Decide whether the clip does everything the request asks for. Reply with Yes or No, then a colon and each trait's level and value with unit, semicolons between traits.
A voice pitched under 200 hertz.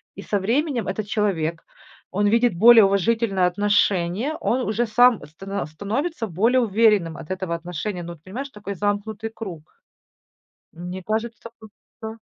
No: high, 205 Hz